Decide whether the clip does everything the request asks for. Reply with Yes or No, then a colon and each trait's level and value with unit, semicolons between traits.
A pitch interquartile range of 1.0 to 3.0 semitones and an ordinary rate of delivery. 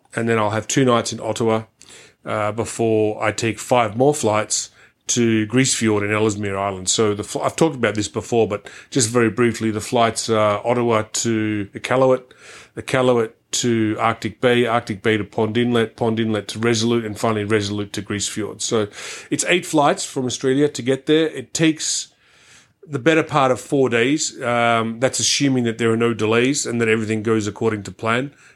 Yes: narrow, 2.4 semitones; average, 185 wpm